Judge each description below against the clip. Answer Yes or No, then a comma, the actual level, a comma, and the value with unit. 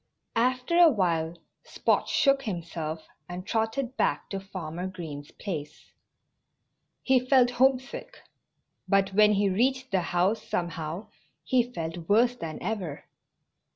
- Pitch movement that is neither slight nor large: No, wide, 6.7 semitones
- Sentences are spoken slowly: Yes, slow, 120 wpm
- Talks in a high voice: Yes, high, 195 Hz